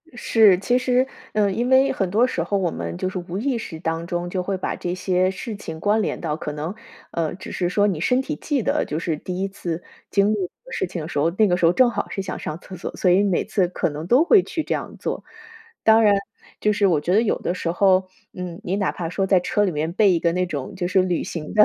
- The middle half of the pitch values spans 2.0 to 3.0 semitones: No, average, 3.6 semitones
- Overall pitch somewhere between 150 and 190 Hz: Yes, medium, 185 Hz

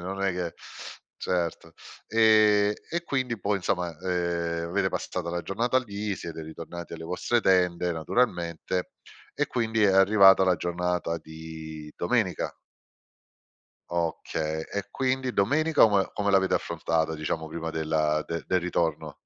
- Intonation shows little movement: No, average, 3.6 semitones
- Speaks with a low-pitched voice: Yes, very low, 90 Hz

